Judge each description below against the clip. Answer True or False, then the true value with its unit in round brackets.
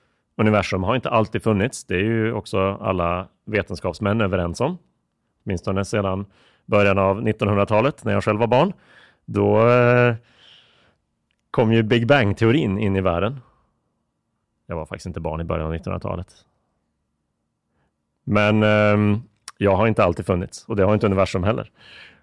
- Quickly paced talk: False (140 wpm)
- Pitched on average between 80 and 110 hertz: True (105 Hz)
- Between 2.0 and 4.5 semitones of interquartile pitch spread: True (2.8 semitones)